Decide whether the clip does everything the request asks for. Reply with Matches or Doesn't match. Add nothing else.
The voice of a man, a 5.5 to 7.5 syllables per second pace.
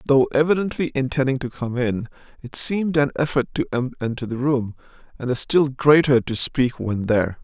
Doesn't match